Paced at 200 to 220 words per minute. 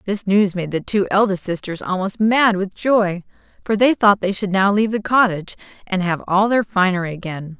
Yes: fast, 205 wpm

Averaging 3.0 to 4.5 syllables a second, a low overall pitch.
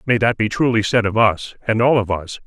No: 5.5 syllables/s; low, 110 Hz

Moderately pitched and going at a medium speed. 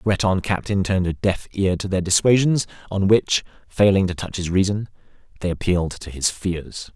No: very low, 95 Hz; average, 190 wpm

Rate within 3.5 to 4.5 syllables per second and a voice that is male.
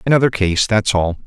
No: 5.5 syllables/s; male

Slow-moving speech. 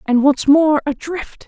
Yes: slow, 120 wpm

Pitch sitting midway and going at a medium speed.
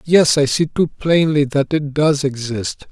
Yes: medium, 145 Hz; average, 185 wpm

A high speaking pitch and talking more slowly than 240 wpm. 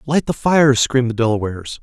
No: low, 125 Hz; average, 200 wpm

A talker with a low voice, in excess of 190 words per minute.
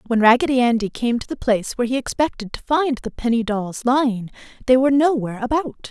No: high, 245 Hz; fast, 205 wpm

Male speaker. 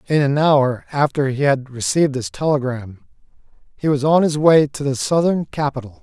Yes: male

